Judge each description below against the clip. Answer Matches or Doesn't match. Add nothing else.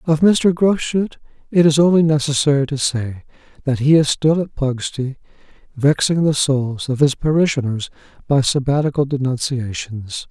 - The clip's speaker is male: Matches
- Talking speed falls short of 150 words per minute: Matches